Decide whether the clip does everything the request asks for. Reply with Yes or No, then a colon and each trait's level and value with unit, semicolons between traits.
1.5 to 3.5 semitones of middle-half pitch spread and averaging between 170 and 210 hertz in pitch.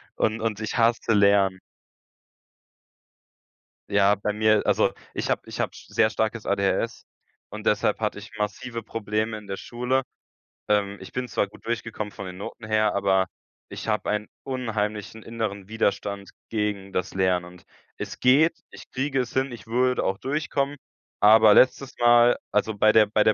No: average, 2.7 semitones; low, 110 Hz